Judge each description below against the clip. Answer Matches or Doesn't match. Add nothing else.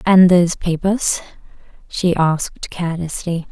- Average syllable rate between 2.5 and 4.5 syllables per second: Matches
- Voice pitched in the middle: Matches